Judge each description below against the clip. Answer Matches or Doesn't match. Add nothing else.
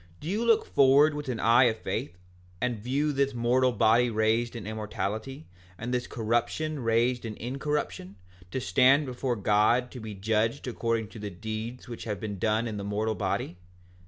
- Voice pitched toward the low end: Matches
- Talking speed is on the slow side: Doesn't match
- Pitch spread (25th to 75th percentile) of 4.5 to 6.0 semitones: Doesn't match